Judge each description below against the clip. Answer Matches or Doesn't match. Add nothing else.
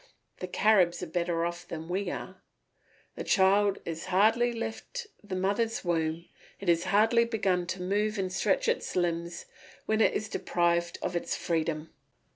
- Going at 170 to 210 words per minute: Doesn't match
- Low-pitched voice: Doesn't match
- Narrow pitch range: Doesn't match